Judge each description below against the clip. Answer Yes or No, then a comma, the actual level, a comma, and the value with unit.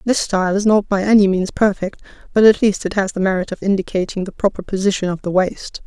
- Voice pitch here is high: Yes, high, 195 Hz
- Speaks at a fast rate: Yes, fast, 235 wpm